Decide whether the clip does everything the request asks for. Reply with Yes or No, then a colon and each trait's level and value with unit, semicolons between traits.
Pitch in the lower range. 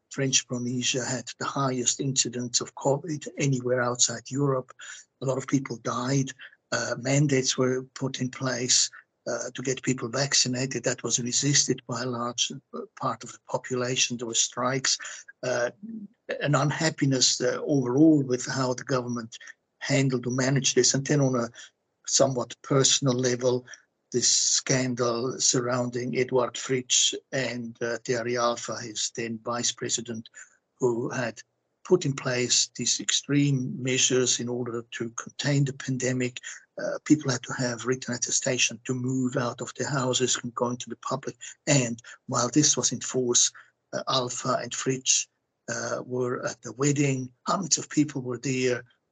Yes: low, 125 Hz